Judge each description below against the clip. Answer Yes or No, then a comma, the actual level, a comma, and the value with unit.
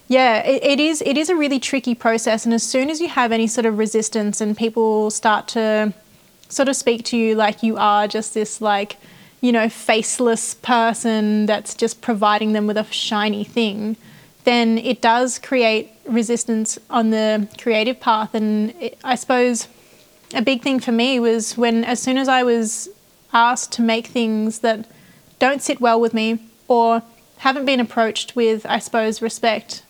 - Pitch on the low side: No, high, 230 Hz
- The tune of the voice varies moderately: No, narrow, 2.1 semitones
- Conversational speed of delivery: Yes, average, 180 wpm